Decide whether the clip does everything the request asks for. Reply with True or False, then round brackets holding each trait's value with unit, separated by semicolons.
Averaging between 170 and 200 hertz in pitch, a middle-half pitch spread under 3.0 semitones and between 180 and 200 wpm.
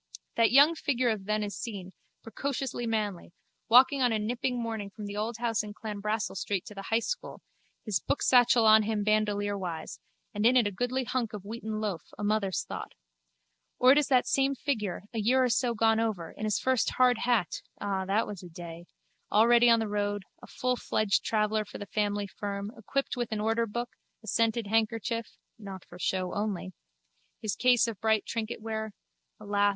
False (220 Hz; 2.6 semitones; 185 wpm)